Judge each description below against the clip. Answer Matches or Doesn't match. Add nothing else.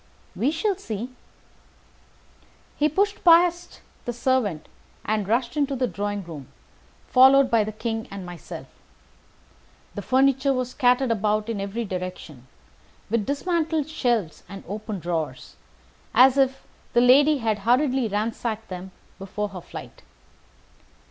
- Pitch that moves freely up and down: Doesn't match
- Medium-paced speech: Doesn't match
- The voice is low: Doesn't match